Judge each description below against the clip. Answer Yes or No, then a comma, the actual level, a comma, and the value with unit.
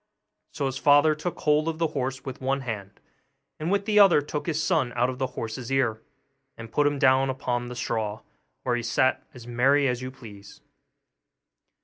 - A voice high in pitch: No, low, 130 Hz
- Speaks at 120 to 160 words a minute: No, average, 195 wpm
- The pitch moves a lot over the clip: No, average, 3.3 semitones